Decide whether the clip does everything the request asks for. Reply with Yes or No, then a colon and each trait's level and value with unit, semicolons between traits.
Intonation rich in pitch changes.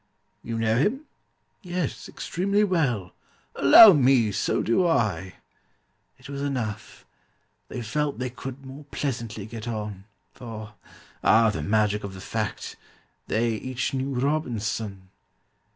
No: average, 4.6 semitones